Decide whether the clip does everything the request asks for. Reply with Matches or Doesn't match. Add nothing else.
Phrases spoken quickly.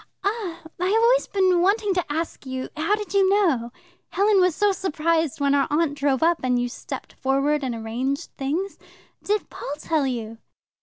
Doesn't match